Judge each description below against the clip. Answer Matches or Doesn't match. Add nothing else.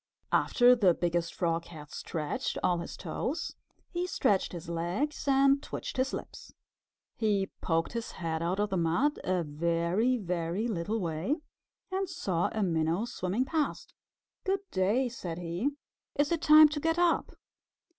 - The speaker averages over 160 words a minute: Doesn't match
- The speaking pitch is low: Doesn't match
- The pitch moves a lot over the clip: Matches